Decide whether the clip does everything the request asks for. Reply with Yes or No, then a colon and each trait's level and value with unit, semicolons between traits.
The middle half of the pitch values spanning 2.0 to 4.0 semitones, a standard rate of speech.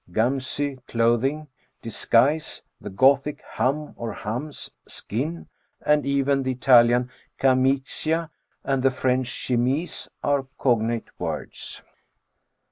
No: average, 2.8 semitones; slow, 100 wpm